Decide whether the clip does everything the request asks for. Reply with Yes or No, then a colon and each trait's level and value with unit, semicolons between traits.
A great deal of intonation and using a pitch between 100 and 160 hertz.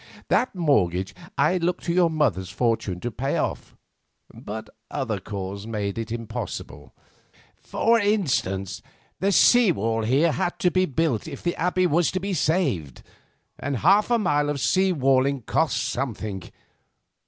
Yes: wide, 8.4 semitones; medium, 140 Hz